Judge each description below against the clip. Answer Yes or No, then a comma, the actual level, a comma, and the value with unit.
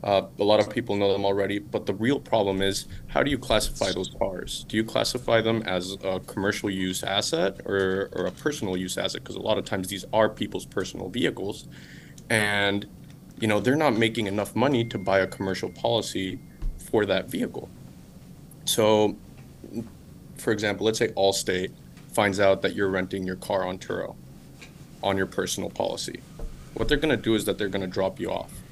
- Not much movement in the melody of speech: Yes, narrow, 2.3 semitones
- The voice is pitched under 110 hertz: Yes, low, 100 Hz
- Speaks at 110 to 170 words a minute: No, average, 190 wpm